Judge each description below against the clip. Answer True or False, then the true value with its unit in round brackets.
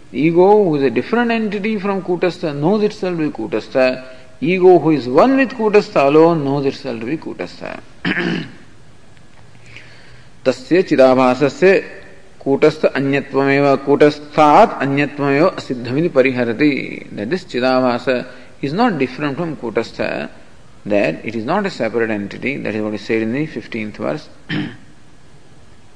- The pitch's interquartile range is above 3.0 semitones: True (5.5 semitones)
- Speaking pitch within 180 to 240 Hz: False (140 Hz)